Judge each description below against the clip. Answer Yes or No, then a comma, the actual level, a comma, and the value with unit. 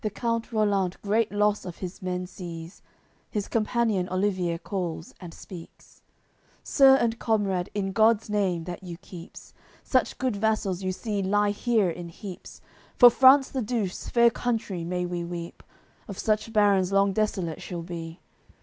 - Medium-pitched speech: No, high, 200 Hz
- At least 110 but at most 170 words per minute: Yes, average, 165 wpm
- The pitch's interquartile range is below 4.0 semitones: Yes, average, 3.5 semitones